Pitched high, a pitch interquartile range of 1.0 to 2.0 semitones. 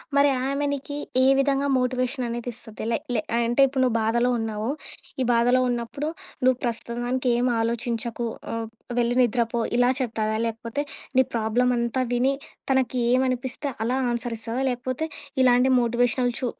Yes: high, 245 Hz; narrow, 1.7 semitones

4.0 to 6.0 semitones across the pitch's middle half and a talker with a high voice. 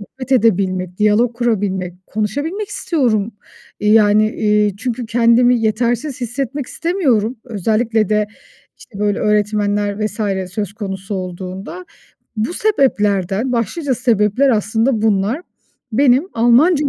No: average, 3.5 semitones; high, 220 Hz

